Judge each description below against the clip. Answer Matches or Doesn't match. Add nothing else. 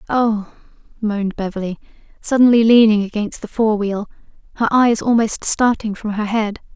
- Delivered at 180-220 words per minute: Doesn't match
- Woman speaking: Matches